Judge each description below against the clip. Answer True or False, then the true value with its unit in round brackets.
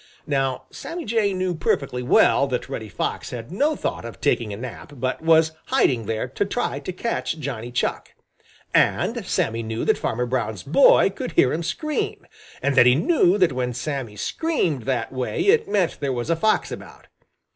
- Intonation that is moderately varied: False (7.1 semitones)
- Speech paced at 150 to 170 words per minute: False (185 wpm)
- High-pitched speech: False (135 Hz)